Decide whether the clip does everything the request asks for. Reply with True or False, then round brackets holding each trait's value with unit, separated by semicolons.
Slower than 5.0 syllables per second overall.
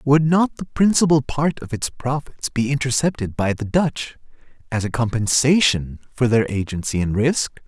True (4.7 syllables/s)